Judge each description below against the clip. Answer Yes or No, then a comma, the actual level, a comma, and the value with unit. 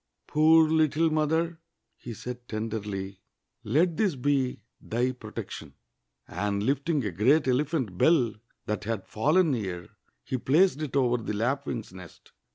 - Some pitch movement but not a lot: No, wide, 6.2 semitones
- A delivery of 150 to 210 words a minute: No, average, 140 wpm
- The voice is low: Yes, low, 130 Hz